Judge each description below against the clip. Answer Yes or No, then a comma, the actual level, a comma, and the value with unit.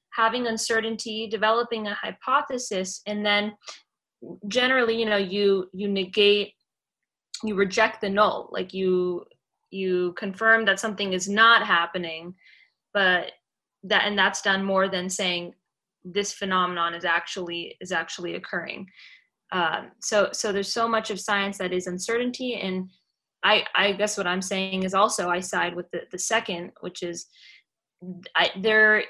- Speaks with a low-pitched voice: No, high, 200 Hz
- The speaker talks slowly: No, average, 145 wpm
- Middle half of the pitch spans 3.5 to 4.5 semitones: No, average, 3.1 semitones